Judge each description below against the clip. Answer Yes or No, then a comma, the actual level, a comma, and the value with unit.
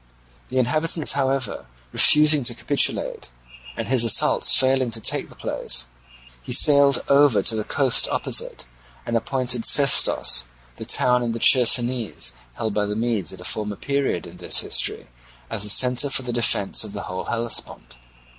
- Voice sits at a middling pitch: No, low, 120 Hz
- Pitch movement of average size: Yes, average, 3.9 semitones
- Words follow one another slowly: No, average, 165 wpm